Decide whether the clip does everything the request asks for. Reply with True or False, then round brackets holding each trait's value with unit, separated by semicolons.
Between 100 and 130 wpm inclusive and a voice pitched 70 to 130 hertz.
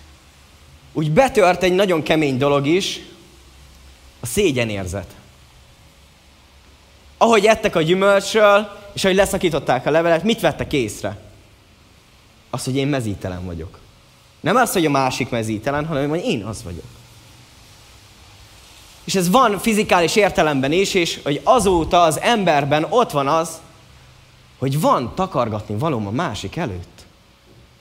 False (125 wpm; 140 Hz)